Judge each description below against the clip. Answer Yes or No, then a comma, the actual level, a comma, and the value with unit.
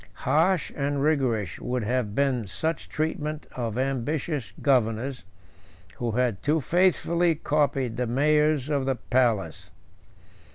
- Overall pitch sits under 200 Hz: Yes, low, 135 Hz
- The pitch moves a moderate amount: Yes, average, 4.1 semitones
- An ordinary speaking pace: No, slow, 120 wpm